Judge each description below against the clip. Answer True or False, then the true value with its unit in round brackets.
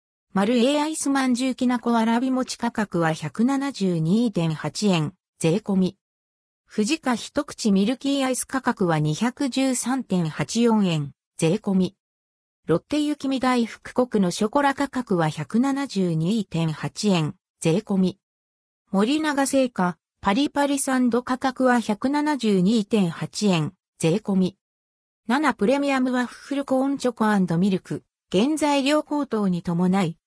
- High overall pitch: True (215 Hz)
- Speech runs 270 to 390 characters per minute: False (210 characters per minute)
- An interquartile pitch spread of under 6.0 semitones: False (6.9 semitones)